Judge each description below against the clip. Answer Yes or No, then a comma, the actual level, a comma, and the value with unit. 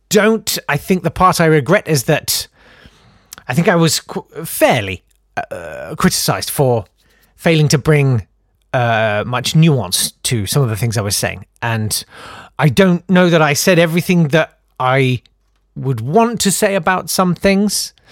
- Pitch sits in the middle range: Yes, medium, 150 Hz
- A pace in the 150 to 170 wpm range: Yes, average, 160 wpm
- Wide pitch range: Yes, wide, 7.5 semitones